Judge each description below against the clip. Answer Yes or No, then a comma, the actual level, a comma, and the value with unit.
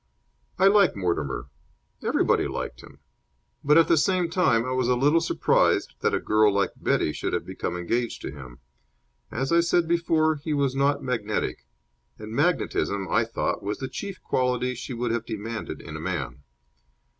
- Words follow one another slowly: No, average, 175 wpm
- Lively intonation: Yes, wide, 6.7 semitones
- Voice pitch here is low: Yes, low, 125 Hz